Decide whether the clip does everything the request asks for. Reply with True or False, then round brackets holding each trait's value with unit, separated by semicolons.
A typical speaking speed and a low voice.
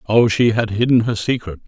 False (215 wpm; 110 Hz)